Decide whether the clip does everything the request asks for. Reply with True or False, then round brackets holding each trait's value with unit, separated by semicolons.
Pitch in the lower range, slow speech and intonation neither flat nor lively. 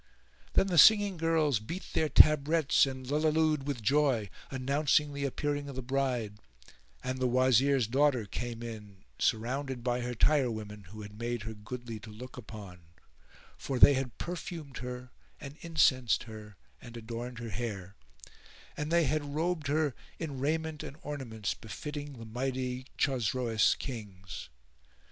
False (130 Hz; 145 wpm; 4.3 semitones)